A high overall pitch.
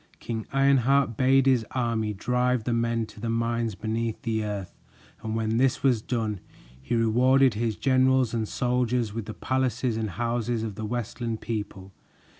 No: low, 115 Hz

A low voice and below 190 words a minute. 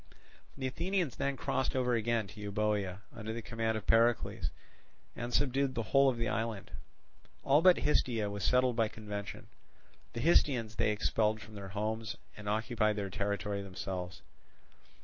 Yes: low, 110 Hz; average, 155 wpm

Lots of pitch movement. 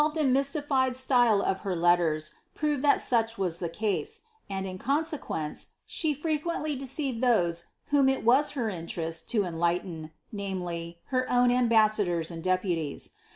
Yes: wide, 7.6 semitones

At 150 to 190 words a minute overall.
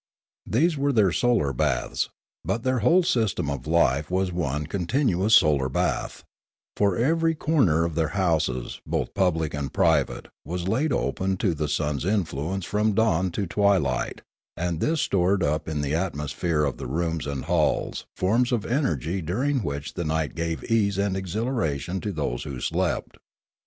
Yes: average, 165 wpm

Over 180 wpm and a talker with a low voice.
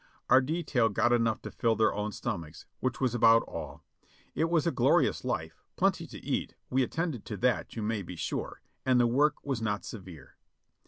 Yes: average, 195 wpm; low, 115 Hz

